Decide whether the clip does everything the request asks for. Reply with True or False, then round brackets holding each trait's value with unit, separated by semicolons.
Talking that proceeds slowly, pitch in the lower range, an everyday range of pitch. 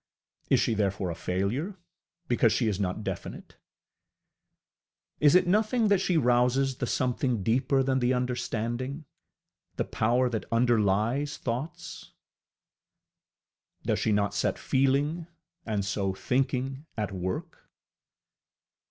True (115 wpm; 125 Hz; 4.2 semitones)